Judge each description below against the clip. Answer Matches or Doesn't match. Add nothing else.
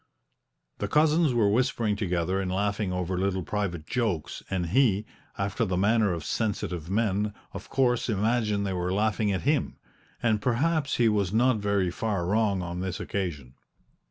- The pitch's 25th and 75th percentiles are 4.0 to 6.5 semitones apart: Doesn't match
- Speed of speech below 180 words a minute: Matches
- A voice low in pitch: Matches